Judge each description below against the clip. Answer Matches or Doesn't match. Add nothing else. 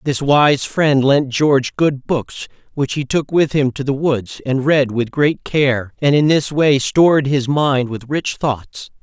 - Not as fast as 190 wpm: Doesn't match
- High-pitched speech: Doesn't match